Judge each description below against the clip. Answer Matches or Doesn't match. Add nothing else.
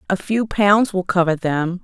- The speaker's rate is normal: Matches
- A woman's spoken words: Matches